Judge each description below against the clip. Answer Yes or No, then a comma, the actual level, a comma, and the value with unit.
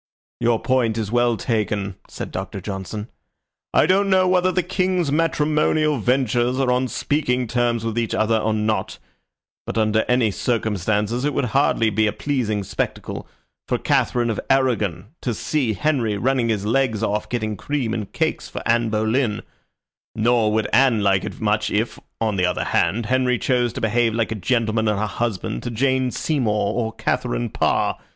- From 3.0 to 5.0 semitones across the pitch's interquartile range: Yes, average, 3.3 semitones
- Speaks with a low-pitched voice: Yes, low, 115 Hz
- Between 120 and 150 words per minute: No, average, 175 wpm